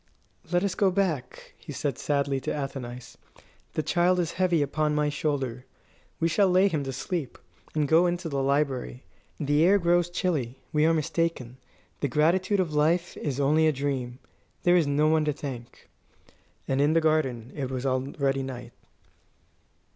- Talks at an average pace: Yes, average, 170 wpm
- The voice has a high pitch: No, medium, 150 Hz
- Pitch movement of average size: Yes, average, 4.0 semitones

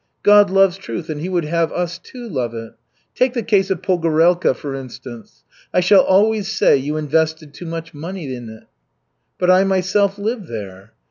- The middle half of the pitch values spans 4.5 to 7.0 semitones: Yes, average, 5.0 semitones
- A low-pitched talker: No, medium, 170 Hz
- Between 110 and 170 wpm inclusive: No, average, 185 wpm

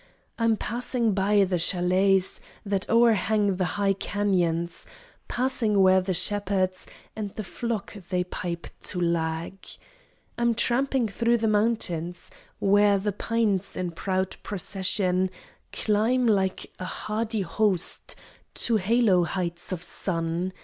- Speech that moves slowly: Yes, slow, 120 wpm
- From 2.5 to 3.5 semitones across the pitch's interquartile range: Yes, average, 3.1 semitones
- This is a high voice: Yes, high, 195 Hz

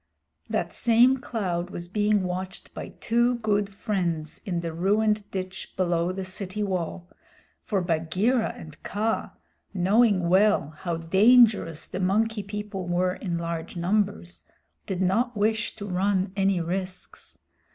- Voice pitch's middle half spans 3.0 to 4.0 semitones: Yes, average, 3.3 semitones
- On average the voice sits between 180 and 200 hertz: Yes, high, 190 Hz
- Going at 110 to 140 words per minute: Yes, slow, 135 wpm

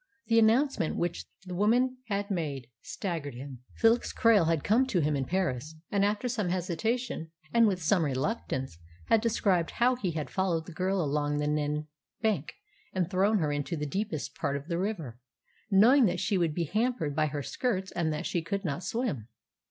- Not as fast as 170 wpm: No, average, 190 wpm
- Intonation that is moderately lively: No, wide, 5.9 semitones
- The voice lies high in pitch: No, medium, 180 Hz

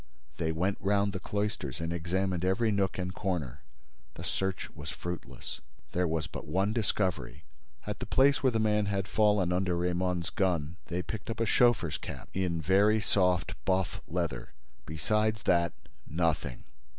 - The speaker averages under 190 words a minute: Yes, average, 160 wpm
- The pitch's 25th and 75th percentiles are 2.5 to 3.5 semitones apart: Yes, average, 3.2 semitones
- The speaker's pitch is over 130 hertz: No, very low, 95 Hz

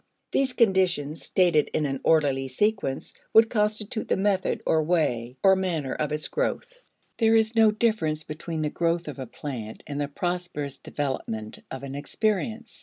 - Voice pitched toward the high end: No, medium, 165 Hz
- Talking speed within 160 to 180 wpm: Yes, average, 165 wpm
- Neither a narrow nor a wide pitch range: No, wide, 6.8 semitones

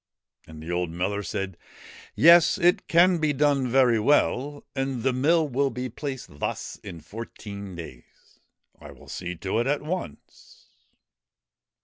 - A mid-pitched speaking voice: No, low, 125 Hz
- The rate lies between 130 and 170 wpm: Yes, average, 150 wpm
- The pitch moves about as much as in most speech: No, wide, 7.3 semitones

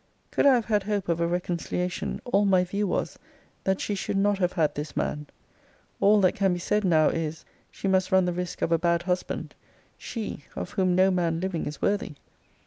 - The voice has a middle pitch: Yes, medium, 180 Hz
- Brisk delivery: Yes, fast, 210 wpm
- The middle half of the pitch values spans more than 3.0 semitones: No, narrow, 2.6 semitones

